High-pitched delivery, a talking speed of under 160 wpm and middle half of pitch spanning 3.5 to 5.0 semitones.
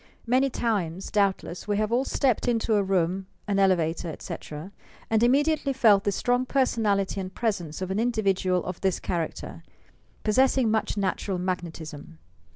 Yes: high, 200 Hz; average, 150 wpm; average, 4.2 semitones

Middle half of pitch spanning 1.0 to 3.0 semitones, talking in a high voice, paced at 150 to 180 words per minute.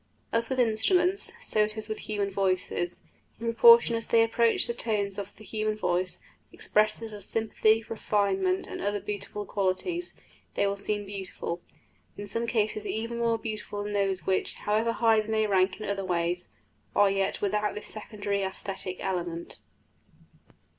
Yes: narrow, 2.4 semitones; high, 210 Hz; average, 160 wpm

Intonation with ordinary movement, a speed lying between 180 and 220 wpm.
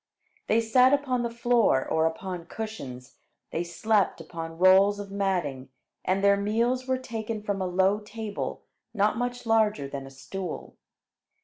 No: average, 4.5 semitones; average, 150 wpm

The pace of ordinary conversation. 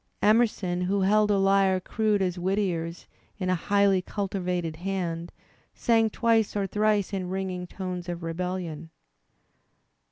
No: slow, 130 wpm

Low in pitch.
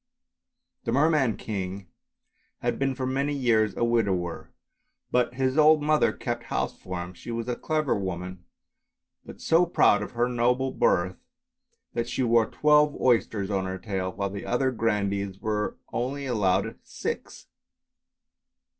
Yes: low, 115 Hz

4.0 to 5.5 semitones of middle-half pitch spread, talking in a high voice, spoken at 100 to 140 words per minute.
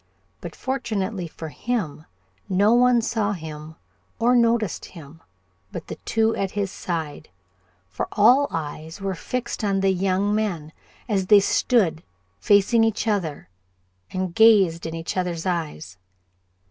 Yes: average, 5.1 semitones; high, 195 Hz; slow, 135 wpm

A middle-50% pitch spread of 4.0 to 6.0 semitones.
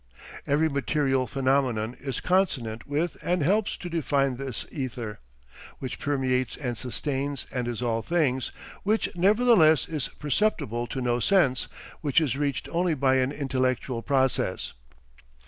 No: average, 3.6 semitones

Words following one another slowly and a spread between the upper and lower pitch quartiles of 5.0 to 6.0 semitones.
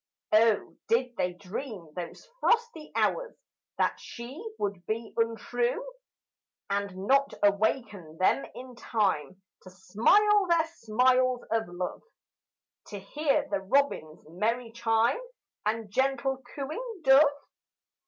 Yes: slow, 115 wpm; average, 5.3 semitones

